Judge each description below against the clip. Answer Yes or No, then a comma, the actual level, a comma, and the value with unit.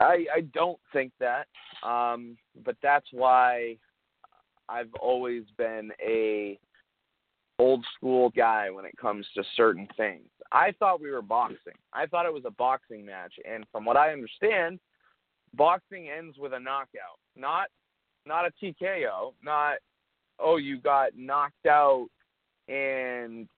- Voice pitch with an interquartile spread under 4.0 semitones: No, average, 4.7 semitones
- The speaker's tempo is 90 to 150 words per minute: Yes, average, 140 wpm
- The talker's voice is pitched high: No, low, 130 Hz